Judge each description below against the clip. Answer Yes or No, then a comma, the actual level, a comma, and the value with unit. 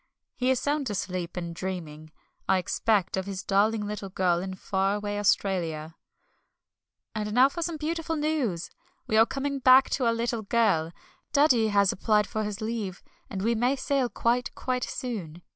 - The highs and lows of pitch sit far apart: No, average, 4.9 semitones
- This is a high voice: Yes, high, 210 Hz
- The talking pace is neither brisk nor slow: Yes, average, 170 wpm